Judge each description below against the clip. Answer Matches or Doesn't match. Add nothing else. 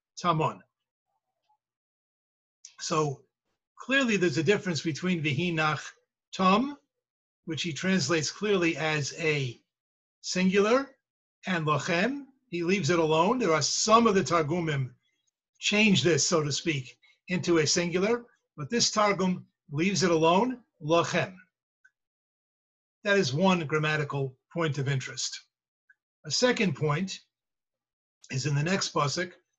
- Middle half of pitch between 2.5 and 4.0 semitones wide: Doesn't match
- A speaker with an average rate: Doesn't match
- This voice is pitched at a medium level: Matches